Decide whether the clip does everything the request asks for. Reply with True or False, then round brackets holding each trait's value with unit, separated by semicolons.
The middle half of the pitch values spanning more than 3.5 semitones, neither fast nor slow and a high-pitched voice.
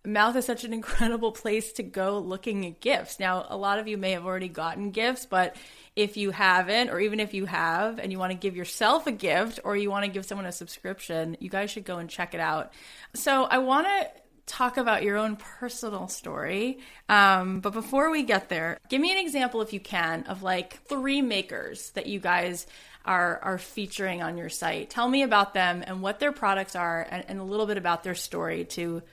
False (3.9 semitones; 220 wpm; 200 Hz)